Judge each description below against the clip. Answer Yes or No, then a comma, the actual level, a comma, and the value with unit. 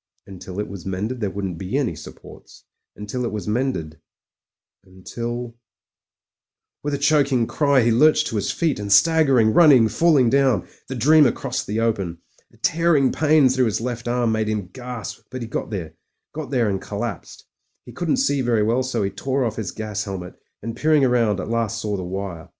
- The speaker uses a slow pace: No, average, 195 wpm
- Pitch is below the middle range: Yes, low, 115 Hz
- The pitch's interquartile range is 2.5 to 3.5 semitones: No, average, 4.7 semitones